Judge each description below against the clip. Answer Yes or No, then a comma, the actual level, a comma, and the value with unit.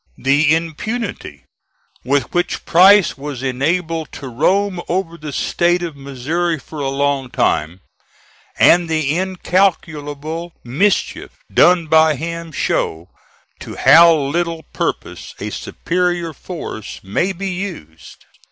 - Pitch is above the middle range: No, medium, 160 Hz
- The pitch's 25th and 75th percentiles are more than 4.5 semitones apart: No, average, 3.9 semitones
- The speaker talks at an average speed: No, slow, 115 wpm